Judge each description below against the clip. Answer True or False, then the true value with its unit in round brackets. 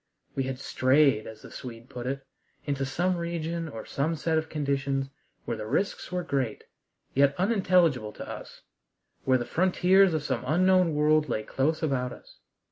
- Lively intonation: False (4.4 semitones)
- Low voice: False (145 Hz)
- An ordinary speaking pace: True (170 wpm)